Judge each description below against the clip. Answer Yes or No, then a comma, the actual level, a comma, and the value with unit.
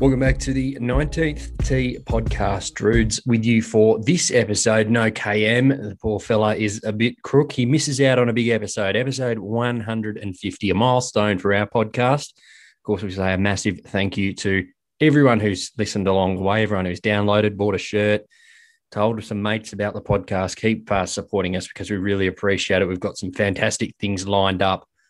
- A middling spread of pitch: Yes, average, 3.3 semitones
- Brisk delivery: No, average, 195 wpm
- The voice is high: No, low, 105 Hz